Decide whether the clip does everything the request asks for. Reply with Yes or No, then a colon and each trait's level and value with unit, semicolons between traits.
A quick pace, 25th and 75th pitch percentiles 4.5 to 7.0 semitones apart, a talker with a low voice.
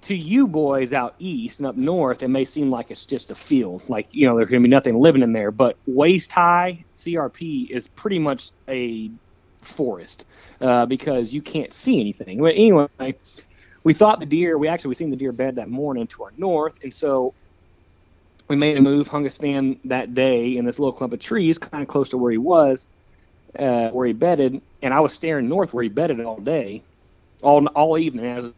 Yes: fast, 215 wpm; average, 4.8 semitones; low, 130 Hz